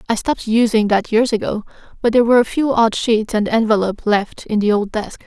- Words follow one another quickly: Yes, fast, 230 wpm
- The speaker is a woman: Yes, female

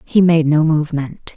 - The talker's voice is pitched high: No, medium, 155 Hz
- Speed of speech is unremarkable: Yes, average, 175 wpm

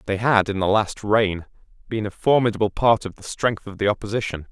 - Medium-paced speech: No, fast, 215 wpm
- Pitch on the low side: Yes, low, 105 Hz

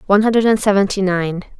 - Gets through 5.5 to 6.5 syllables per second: Yes, 6.2 syllables/s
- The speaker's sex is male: No, female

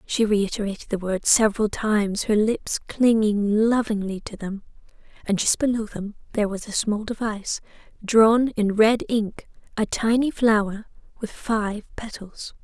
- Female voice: Yes, female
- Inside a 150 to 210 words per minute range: No, average, 140 wpm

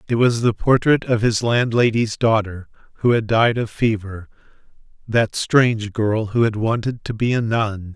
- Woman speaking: No, male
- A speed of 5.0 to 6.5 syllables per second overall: No, 4.5 syllables/s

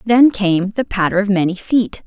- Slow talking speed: No, fast, 205 wpm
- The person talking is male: No, female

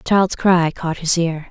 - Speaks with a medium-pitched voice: Yes, medium, 170 Hz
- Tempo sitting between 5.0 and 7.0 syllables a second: No, 4.1 syllables/s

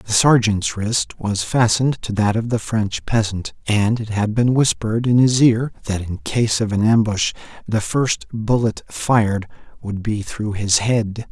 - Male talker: Yes, male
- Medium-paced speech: Yes, average, 180 wpm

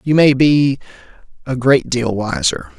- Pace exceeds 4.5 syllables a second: No, 4.0 syllables/s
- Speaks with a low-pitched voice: Yes, low, 125 Hz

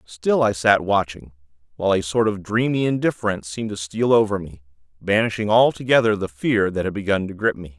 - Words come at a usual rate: Yes, average, 195 wpm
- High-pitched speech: No, low, 100 Hz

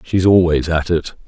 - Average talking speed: Yes, average, 190 wpm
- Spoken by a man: Yes, male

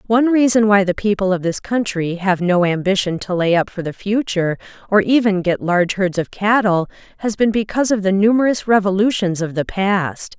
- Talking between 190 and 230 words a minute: Yes, average, 195 wpm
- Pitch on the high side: Yes, high, 195 Hz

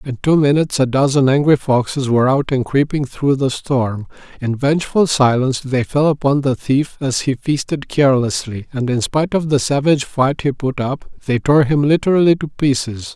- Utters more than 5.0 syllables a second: Yes, 5.2 syllables/s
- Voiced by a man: Yes, male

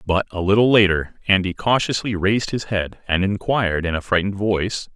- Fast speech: No, average, 180 wpm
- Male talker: Yes, male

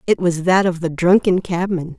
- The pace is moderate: No, fast, 210 wpm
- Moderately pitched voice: Yes, medium, 175 Hz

